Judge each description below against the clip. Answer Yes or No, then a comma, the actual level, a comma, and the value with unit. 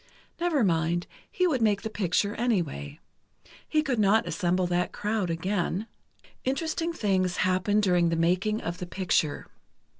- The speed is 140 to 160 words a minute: Yes, average, 145 wpm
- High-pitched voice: Yes, high, 195 Hz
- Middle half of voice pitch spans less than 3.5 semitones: No, average, 4.0 semitones